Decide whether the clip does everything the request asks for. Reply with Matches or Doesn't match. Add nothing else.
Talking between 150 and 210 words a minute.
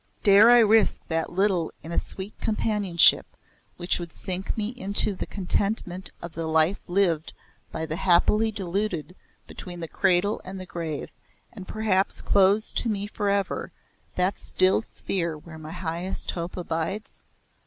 Matches